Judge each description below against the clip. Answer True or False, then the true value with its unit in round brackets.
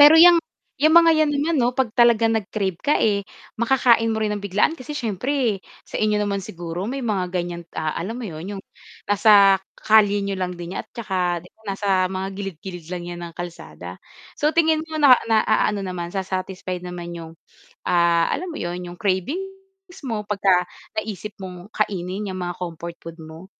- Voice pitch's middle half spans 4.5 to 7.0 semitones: True (4.9 semitones)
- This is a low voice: False (200 Hz)